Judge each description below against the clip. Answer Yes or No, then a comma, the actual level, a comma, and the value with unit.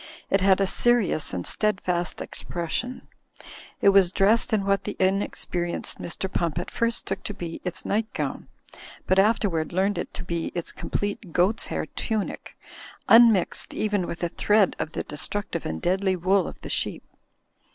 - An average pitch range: Yes, average, 3.0 semitones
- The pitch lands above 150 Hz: Yes, high, 190 Hz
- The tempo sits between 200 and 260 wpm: No, average, 170 wpm